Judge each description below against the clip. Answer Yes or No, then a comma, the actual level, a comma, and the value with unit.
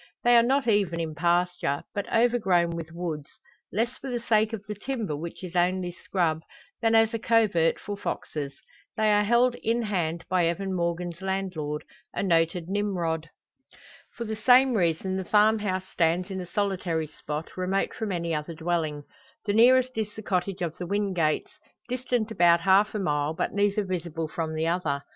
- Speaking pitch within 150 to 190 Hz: Yes, medium, 185 Hz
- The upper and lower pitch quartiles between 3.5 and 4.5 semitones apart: Yes, average, 4.2 semitones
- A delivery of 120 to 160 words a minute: No, average, 180 wpm